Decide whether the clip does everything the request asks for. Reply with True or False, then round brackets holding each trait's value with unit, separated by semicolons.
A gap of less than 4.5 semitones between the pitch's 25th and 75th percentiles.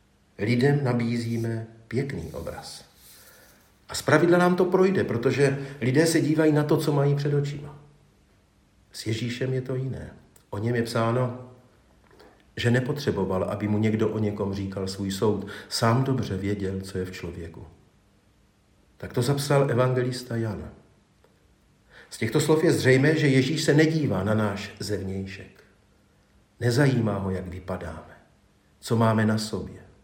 False (5.6 semitones)